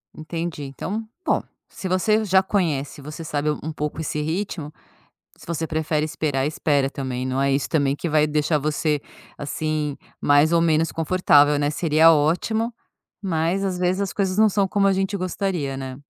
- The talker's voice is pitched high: No, medium, 155 Hz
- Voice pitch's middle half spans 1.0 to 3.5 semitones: No, average, 4.0 semitones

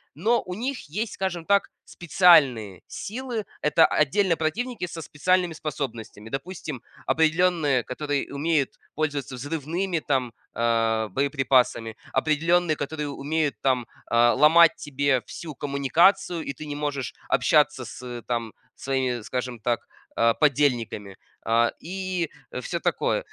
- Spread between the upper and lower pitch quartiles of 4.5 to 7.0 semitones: Yes, average, 5.1 semitones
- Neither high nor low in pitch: Yes, medium, 145 Hz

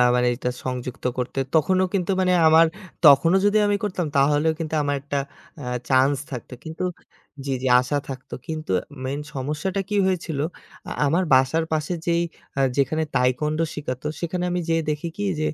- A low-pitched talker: No, medium, 155 Hz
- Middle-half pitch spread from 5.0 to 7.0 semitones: No, average, 4.0 semitones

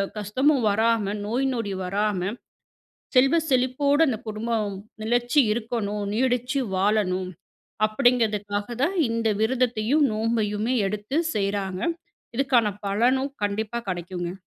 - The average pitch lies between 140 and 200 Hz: No, high, 220 Hz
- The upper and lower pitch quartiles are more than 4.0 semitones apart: No, average, 3.5 semitones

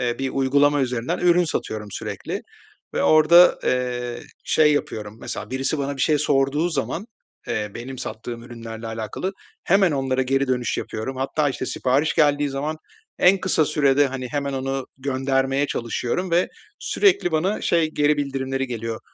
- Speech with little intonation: No, average, 3.2 semitones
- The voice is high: No, low, 135 Hz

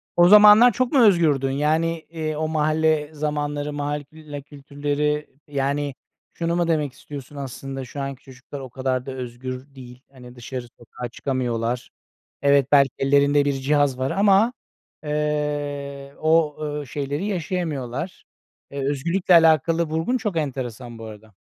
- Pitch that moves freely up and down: No, average, 2.9 semitones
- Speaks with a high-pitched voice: No, medium, 145 Hz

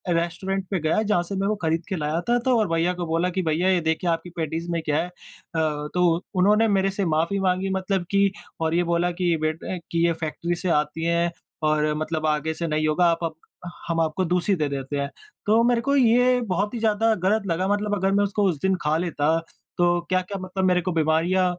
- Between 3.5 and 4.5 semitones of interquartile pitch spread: No, average, 3.1 semitones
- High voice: No, medium, 175 Hz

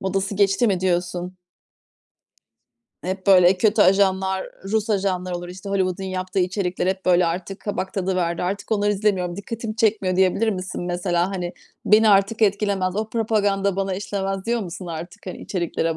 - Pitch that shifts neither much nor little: No, narrow, 1.9 semitones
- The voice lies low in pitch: No, high, 190 Hz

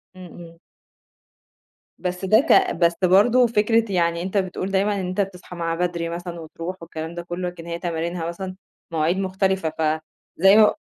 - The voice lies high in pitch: No, medium, 180 Hz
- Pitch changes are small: Yes, narrow, 2.2 semitones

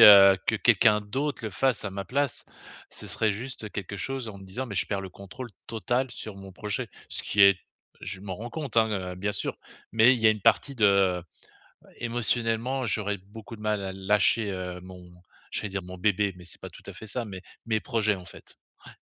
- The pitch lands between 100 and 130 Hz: Yes, low, 105 Hz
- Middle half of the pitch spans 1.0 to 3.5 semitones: Yes, average, 3.0 semitones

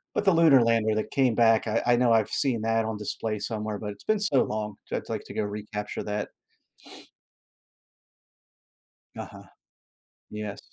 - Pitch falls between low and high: No, low, 110 Hz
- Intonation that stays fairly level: Yes, narrow, 2.2 semitones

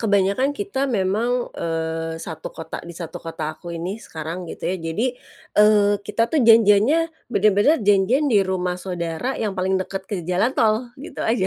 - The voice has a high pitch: Yes, high, 195 Hz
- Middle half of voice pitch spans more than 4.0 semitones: Yes, average, 4.5 semitones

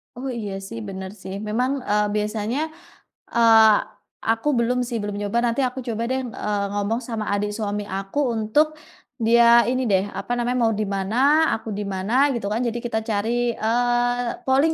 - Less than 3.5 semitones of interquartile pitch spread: Yes, average, 2.9 semitones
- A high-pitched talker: Yes, high, 230 Hz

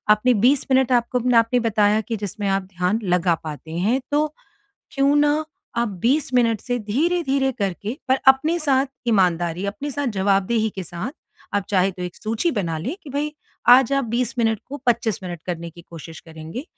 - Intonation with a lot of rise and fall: Yes, wide, 6.1 semitones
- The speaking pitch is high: Yes, high, 230 Hz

